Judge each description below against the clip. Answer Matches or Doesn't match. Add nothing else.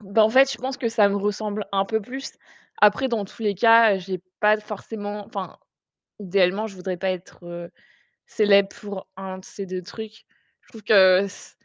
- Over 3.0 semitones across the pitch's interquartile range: Doesn't match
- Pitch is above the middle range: Matches